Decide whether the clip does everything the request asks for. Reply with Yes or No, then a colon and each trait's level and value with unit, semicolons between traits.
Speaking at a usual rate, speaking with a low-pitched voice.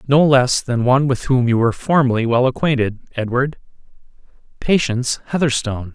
No: slow, 130 wpm; low, 125 Hz